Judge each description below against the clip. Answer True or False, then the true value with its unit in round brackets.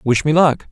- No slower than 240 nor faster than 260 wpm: True (255 wpm)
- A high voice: False (145 Hz)